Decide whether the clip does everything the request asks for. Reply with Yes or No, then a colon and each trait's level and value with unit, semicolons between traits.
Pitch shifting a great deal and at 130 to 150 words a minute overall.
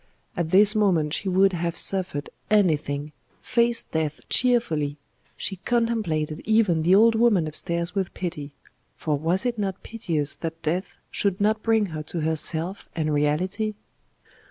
No: average, 5.0 semitones; average, 145 wpm